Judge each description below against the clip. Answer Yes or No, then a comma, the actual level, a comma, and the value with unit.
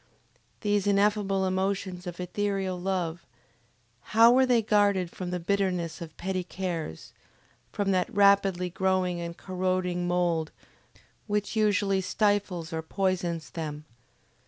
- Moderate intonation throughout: No, narrow, 2.3 semitones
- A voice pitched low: No, medium, 185 Hz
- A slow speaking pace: Yes, slow, 120 wpm